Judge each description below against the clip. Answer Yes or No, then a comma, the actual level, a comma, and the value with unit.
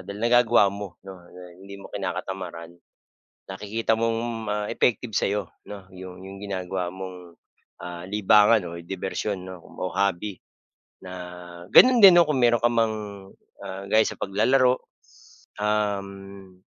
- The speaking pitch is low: Yes, low, 100 Hz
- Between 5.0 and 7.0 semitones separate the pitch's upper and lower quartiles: No, average, 2.9 semitones